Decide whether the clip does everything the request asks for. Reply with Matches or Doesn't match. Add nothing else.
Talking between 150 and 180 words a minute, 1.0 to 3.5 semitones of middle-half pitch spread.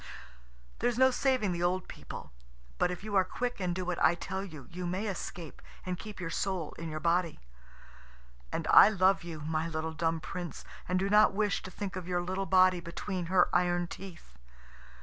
Doesn't match